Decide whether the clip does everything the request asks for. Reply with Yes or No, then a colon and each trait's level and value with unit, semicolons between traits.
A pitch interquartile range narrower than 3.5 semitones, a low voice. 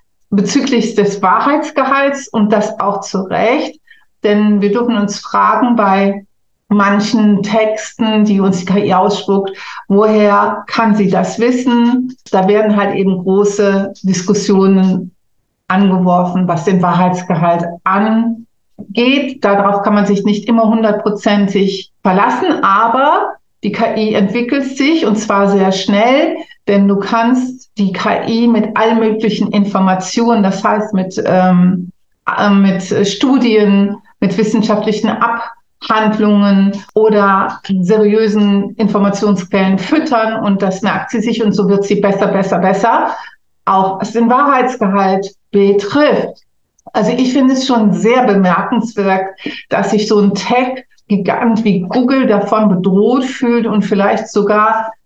No: narrow, 2.6 semitones; high, 210 Hz